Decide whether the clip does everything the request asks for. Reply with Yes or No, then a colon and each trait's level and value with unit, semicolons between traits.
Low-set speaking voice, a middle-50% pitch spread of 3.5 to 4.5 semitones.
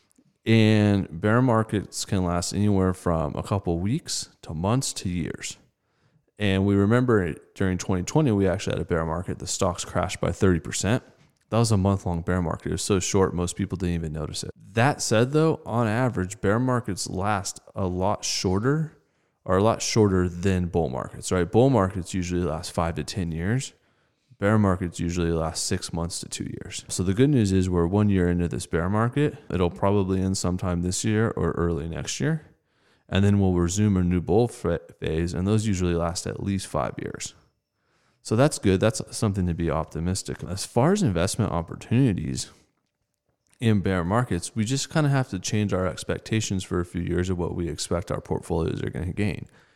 Yes: very low, 95 Hz; average, 3.9 semitones